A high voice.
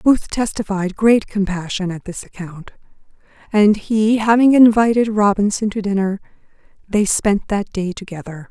Yes: high, 205 Hz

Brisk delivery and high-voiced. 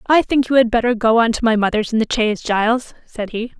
Yes: fast, 265 wpm; high, 230 Hz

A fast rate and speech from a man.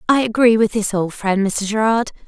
No: fast, 210 wpm; female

